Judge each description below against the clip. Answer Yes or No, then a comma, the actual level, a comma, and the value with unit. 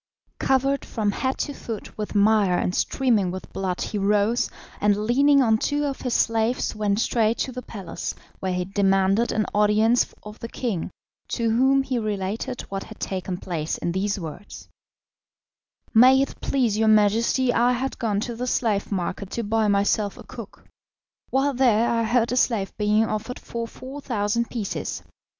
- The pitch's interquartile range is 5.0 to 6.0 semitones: No, average, 3.5 semitones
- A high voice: Yes, high, 220 Hz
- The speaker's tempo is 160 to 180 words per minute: Yes, average, 170 wpm